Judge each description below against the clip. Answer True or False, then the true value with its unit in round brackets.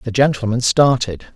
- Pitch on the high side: False (120 Hz)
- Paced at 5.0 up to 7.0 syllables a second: True (5.2 syllables/s)